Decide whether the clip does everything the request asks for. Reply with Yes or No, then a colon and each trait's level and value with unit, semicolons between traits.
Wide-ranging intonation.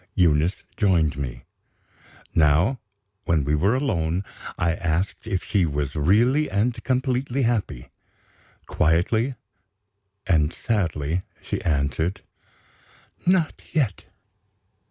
Yes: wide, 7.1 semitones